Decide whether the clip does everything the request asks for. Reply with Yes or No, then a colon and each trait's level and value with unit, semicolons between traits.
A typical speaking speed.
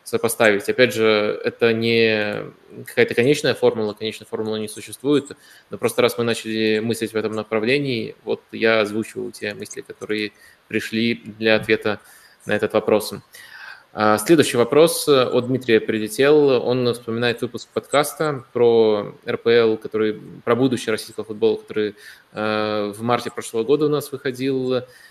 Yes: average, 135 wpm